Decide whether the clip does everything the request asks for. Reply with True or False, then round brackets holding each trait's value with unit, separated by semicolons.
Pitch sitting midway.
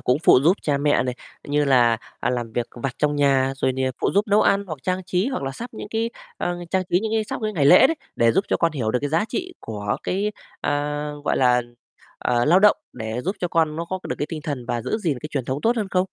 True (150 Hz)